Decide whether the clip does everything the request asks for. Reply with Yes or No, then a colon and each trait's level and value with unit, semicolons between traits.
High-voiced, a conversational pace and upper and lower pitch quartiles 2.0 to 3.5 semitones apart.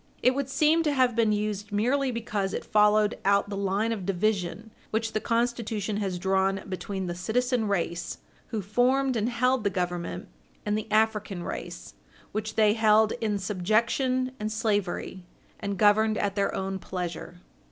Yes: high, 210 Hz; average, 165 wpm; average, 2.8 semitones